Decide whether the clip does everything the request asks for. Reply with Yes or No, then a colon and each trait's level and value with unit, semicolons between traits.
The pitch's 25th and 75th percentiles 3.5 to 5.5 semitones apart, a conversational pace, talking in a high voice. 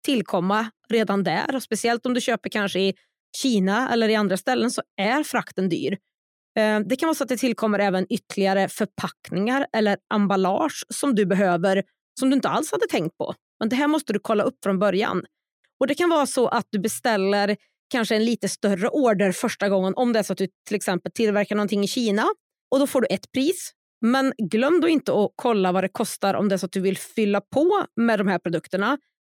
No: average, 4.4 semitones; fast, 215 wpm; high, 215 Hz